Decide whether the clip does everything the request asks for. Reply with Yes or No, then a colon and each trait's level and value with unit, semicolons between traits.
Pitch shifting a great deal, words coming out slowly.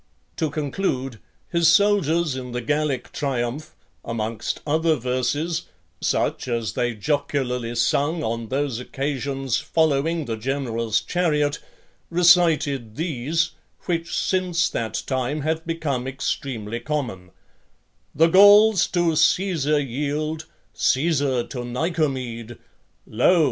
No: average, 4.8 semitones; slow, 105 wpm